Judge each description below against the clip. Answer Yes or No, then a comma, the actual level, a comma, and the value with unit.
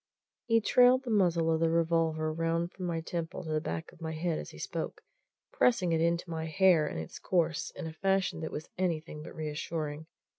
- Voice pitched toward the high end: No, medium, 165 Hz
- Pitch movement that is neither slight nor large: No, narrow, 2.1 semitones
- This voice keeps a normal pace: No, fast, 210 wpm